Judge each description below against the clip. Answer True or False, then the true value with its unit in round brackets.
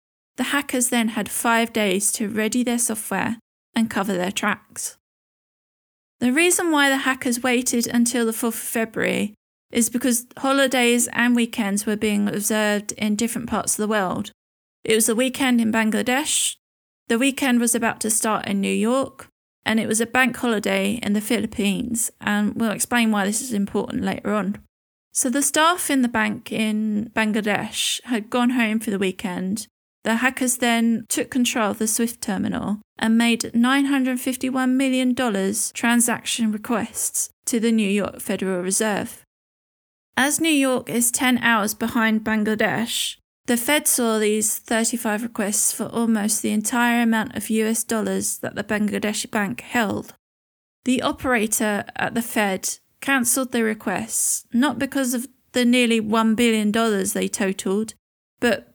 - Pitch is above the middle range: True (230 Hz)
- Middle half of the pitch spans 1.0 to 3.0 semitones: True (2.5 semitones)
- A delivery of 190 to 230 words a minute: False (155 wpm)